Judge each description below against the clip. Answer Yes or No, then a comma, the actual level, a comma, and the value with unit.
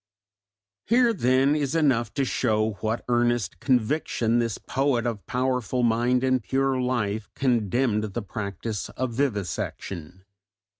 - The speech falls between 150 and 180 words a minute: No, slow, 135 wpm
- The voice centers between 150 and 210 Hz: No, low, 120 Hz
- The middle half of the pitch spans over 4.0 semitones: No, average, 3.4 semitones